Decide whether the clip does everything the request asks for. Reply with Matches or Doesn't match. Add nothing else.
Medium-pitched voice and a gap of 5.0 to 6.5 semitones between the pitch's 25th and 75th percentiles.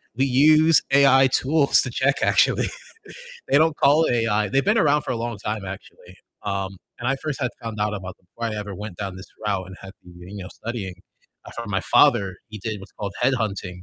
Doesn't match